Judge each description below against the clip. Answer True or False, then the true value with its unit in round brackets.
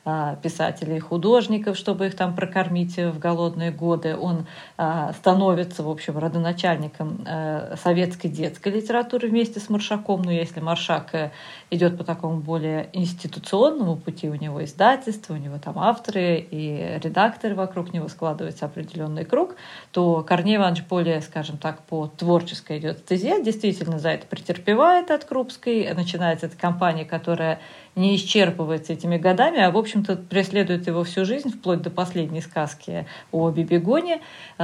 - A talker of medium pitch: True (175 Hz)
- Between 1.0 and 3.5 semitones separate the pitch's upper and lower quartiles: True (3.0 semitones)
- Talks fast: False (135 wpm)